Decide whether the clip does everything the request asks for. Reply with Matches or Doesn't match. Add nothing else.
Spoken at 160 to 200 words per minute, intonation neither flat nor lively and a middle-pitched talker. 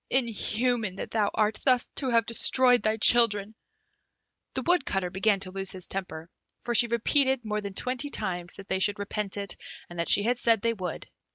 Doesn't match